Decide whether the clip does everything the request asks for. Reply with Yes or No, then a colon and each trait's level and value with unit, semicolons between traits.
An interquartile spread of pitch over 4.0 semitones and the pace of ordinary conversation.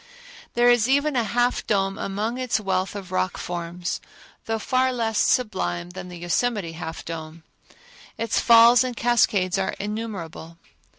Yes: average, 5.2 semitones; average, 145 wpm